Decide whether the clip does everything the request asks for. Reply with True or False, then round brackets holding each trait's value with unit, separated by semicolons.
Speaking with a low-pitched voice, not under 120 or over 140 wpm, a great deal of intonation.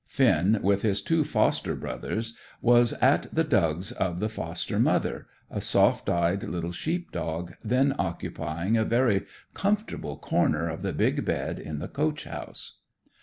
False (105 Hz; 155 wpm; 7.3 semitones)